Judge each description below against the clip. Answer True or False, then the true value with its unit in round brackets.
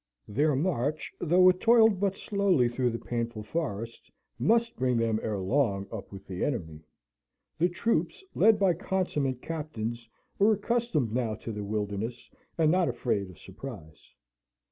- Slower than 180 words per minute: True (150 wpm)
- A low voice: True (130 Hz)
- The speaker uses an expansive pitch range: True (8.8 semitones)